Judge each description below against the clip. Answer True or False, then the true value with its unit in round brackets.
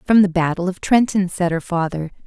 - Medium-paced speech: False (210 wpm)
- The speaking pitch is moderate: True (180 Hz)